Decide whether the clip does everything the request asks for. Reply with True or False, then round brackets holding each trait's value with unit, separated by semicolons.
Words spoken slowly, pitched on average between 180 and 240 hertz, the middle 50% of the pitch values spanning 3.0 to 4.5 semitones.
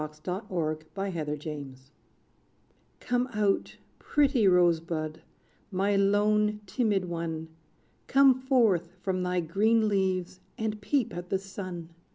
True (125 wpm; 190 Hz; 4.0 semitones)